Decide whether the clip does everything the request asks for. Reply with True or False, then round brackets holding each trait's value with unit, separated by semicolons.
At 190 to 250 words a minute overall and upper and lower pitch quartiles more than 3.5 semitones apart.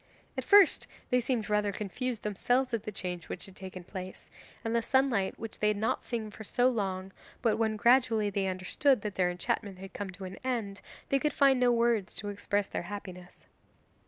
True (200 wpm; 3.9 semitones)